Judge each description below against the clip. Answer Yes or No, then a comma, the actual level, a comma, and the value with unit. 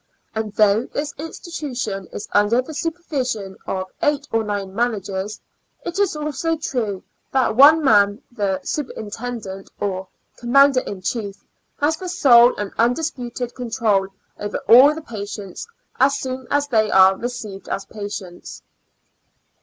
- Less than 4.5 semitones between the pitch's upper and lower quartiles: No, wide, 5.5 semitones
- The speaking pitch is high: Yes, high, 235 Hz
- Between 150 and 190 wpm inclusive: No, slow, 135 wpm